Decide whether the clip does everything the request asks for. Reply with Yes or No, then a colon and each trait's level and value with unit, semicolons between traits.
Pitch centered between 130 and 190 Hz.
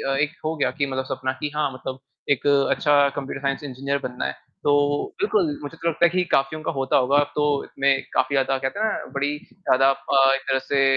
Yes: medium, 140 Hz